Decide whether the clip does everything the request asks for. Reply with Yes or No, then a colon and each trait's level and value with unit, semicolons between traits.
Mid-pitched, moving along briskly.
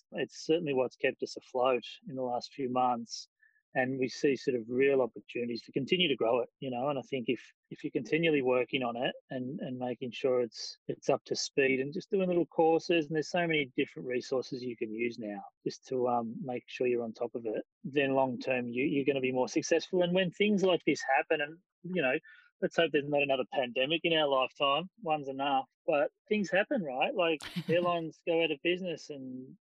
Yes: medium, 145 Hz; fast, 220 wpm